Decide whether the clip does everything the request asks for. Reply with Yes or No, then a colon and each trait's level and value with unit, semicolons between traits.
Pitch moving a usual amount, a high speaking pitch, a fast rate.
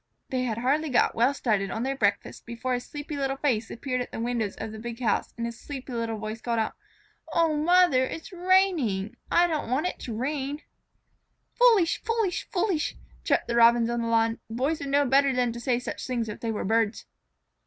Yes: average, 4.3 semitones; very high, 250 Hz; fast, 210 wpm